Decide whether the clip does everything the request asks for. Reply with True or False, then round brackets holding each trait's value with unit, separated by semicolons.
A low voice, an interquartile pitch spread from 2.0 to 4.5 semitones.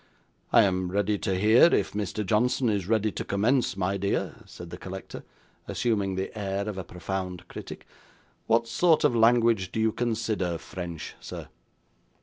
True (100 Hz; 3.2 semitones)